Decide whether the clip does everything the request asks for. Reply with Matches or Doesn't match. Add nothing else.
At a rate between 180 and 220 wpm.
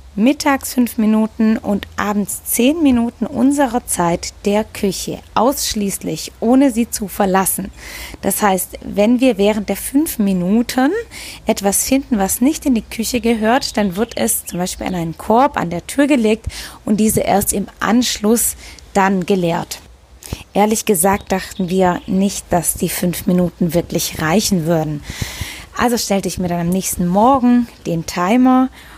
Doesn't match